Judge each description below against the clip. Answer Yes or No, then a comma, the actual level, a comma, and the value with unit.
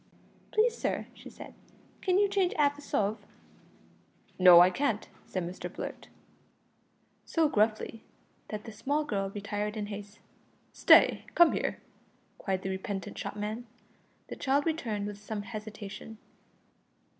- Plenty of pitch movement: Yes, wide, 5.8 semitones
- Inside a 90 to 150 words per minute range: Yes, slow, 135 wpm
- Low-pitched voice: No, high, 215 Hz